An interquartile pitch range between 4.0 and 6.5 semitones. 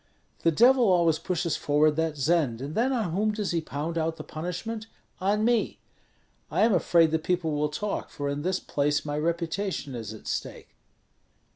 Yes: average, 4.9 semitones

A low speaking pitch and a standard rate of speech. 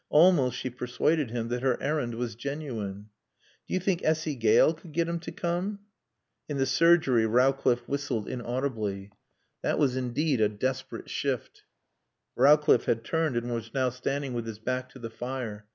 Yes: low, 130 Hz; average, 170 wpm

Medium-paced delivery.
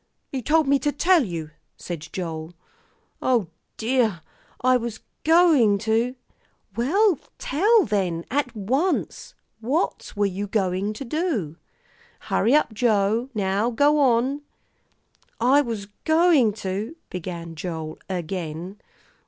No: slow, 125 wpm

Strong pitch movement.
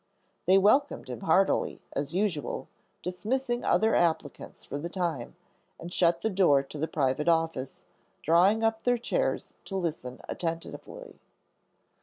Yes: wide, 5.7 semitones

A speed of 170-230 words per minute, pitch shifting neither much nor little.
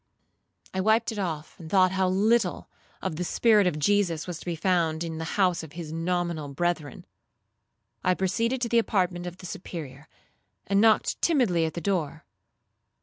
Yes: average, 175 wpm; average, 3.6 semitones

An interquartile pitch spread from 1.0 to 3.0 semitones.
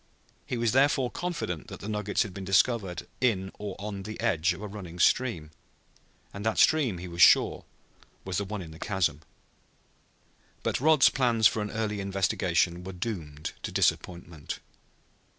No: average, 4.1 semitones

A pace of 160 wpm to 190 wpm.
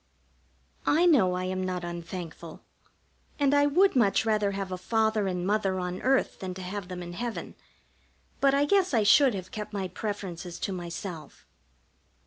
Yes: average, 170 wpm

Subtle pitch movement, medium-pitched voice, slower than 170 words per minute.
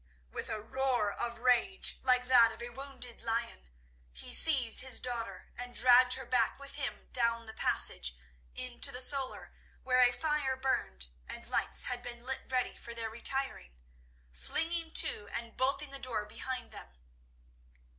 No: narrow, 2.3 semitones; high, 245 Hz; average, 160 wpm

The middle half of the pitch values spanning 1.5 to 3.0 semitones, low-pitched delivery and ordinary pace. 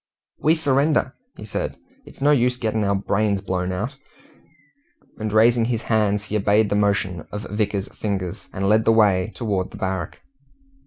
Yes: average, 2.7 semitones; low, 105 Hz; average, 165 wpm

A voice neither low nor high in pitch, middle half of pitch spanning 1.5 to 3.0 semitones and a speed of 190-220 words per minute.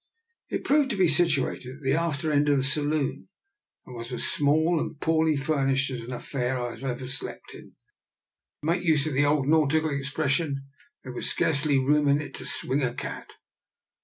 Yes: medium, 145 Hz; average, 2.7 semitones; average, 195 wpm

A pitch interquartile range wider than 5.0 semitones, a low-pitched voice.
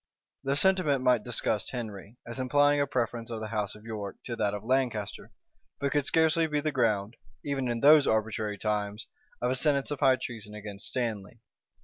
No: average, 4.6 semitones; low, 120 Hz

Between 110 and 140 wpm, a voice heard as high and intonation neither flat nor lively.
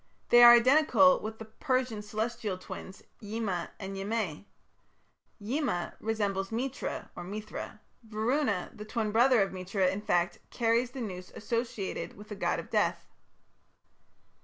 Yes: slow, 135 wpm; high, 215 Hz; average, 3.4 semitones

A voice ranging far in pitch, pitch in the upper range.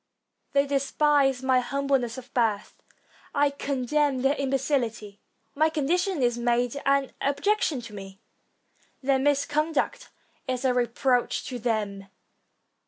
No: average, 2.8 semitones; very high, 270 Hz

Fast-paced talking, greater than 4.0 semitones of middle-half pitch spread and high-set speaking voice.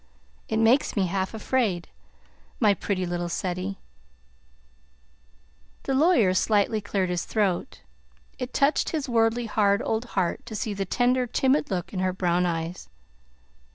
No: average, 140 wpm; average, 4.5 semitones; high, 205 Hz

